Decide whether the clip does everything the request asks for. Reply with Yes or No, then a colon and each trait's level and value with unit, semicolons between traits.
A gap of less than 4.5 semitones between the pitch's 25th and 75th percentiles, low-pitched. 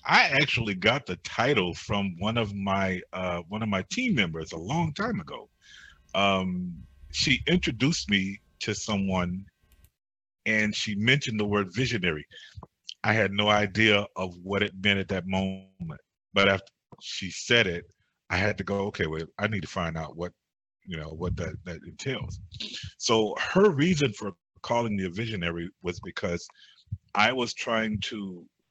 Yes: average, 3.5 semitones; low, 100 Hz